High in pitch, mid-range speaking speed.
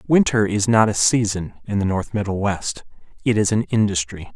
No: low, 105 Hz; average, 180 wpm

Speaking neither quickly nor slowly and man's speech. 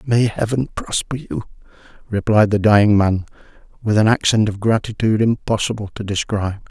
Yes: average, 145 wpm; male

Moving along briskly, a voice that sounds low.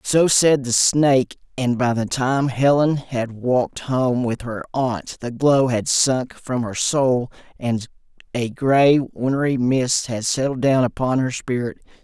No: average, 165 wpm; low, 125 Hz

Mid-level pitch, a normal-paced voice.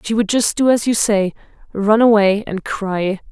No: high, 210 Hz; average, 180 wpm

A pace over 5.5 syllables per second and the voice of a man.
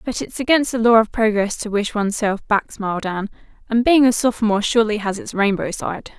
No: 6.0 syllables/s; female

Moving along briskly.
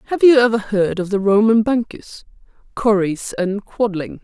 No: average, 155 wpm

